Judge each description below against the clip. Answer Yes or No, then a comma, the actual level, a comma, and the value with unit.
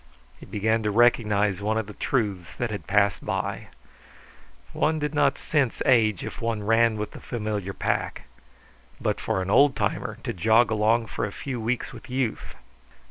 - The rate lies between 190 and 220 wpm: No, average, 175 wpm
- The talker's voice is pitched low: Yes, low, 110 Hz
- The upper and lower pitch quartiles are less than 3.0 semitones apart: Yes, narrow, 2.5 semitones